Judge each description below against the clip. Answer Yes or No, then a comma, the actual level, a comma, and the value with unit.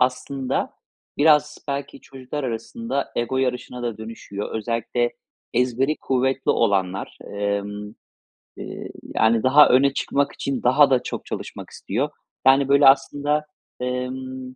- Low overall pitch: Yes, low, 130 Hz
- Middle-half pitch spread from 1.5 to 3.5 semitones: Yes, average, 3.0 semitones